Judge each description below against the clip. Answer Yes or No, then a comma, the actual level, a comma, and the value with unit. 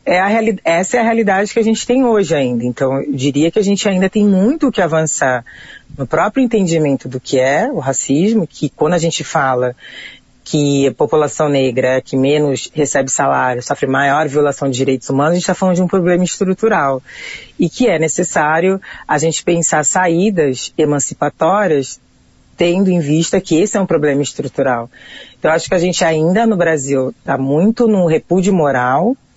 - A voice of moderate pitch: Yes, medium, 160 Hz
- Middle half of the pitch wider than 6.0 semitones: No, wide, 5.5 semitones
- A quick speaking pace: Yes, fast, 190 wpm